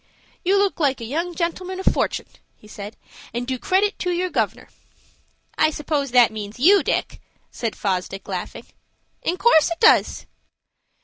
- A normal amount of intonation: No, wide, 8.2 semitones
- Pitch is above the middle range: Yes, very high, 305 Hz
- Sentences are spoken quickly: No, average, 160 wpm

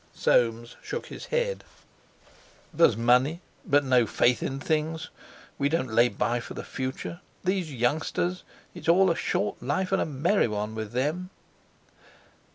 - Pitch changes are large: Yes, wide, 5.9 semitones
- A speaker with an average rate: Yes, average, 145 wpm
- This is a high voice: No, medium, 140 Hz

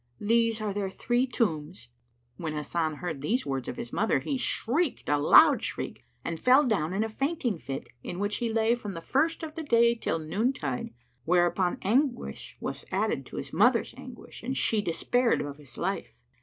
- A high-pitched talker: Yes, high, 210 Hz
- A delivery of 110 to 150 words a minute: No, average, 190 wpm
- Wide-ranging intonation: Yes, wide, 6.9 semitones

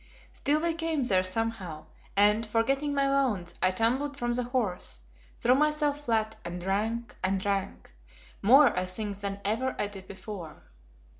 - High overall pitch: Yes, high, 225 Hz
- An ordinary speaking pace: Yes, average, 155 wpm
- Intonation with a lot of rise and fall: Yes, wide, 5.7 semitones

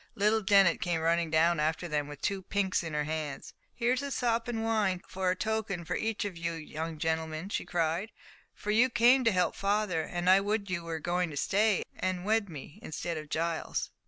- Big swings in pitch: No, average, 4.5 semitones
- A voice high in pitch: No, medium, 180 Hz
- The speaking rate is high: Yes, fast, 210 wpm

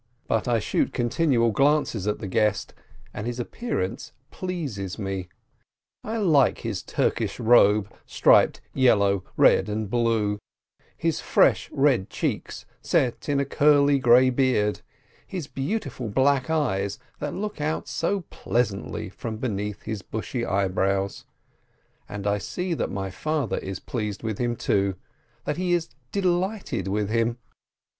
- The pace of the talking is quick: No, slow, 135 wpm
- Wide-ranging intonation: Yes, wide, 5.8 semitones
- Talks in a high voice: No, low, 115 Hz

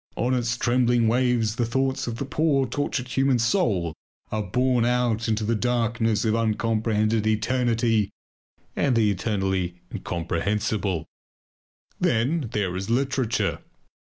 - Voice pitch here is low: Yes, low, 115 Hz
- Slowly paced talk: Yes, slow, 125 wpm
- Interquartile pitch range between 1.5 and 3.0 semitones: Yes, narrow, 2.6 semitones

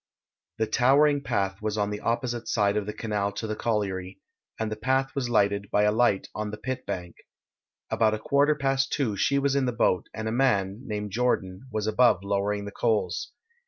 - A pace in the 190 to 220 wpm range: Yes, average, 200 wpm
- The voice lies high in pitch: No, low, 110 Hz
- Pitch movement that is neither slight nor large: Yes, average, 3.7 semitones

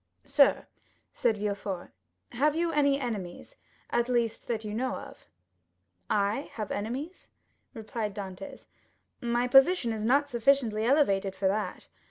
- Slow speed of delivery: Yes, slow, 125 wpm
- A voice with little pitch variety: No, average, 4.5 semitones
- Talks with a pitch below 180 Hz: No, high, 230 Hz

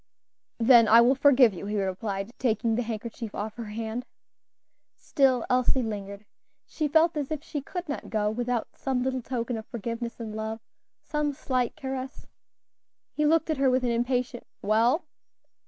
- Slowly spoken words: No, average, 165 wpm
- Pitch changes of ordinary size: Yes, average, 3.3 semitones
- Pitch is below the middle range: No, high, 240 Hz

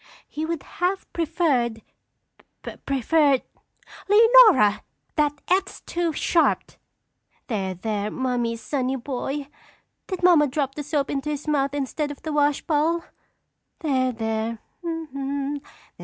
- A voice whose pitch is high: Yes, very high, 285 Hz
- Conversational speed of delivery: No, slow, 125 wpm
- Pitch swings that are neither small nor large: Yes, average, 4.1 semitones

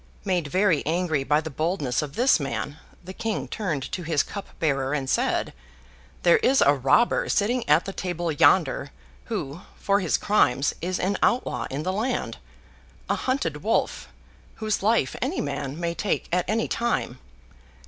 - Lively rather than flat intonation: Yes, wide, 5.7 semitones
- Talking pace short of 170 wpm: Yes, average, 160 wpm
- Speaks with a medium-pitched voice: Yes, medium, 175 Hz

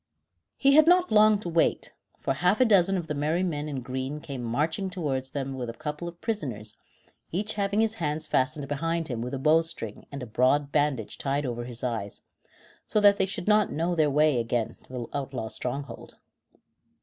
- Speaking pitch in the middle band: Yes, medium, 150 Hz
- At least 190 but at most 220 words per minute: Yes, average, 200 wpm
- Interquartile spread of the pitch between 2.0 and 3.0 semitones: No, wide, 5.6 semitones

